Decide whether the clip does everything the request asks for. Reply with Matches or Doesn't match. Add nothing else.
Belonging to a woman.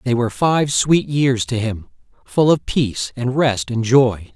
Doesn't match